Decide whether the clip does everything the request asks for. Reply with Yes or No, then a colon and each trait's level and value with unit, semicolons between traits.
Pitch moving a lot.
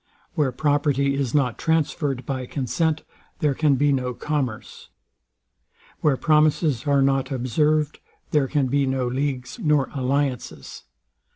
No: narrow, 2.4 semitones